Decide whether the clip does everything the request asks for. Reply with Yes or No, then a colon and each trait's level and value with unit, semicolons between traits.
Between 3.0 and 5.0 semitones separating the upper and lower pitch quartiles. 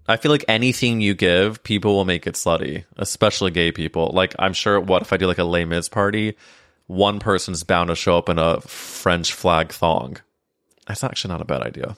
Yes: average, 3.3 semitones